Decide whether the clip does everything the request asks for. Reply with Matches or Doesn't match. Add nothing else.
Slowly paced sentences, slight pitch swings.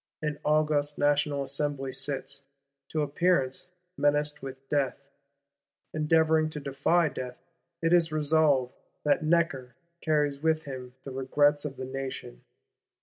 Matches